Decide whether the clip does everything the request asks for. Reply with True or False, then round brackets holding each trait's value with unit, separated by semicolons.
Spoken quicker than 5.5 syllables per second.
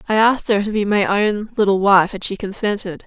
True (5.7 syllables/s)